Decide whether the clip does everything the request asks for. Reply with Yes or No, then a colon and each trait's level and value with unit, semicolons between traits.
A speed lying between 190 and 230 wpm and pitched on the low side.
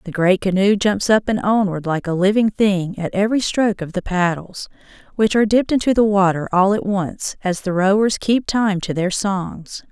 No: fast, 205 wpm; high, 195 Hz